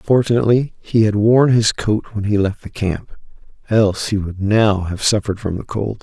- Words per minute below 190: No, average, 200 wpm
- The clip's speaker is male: Yes, male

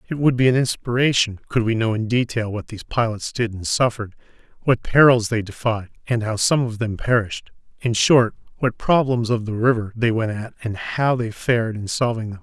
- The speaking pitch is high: No, low, 115 Hz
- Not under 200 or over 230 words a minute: Yes, fast, 205 wpm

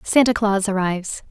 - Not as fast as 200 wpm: Yes, average, 140 wpm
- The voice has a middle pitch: No, high, 205 Hz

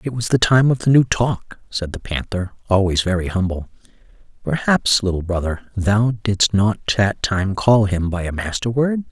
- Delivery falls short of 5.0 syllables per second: Yes, 4.4 syllables/s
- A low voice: Yes, low, 105 Hz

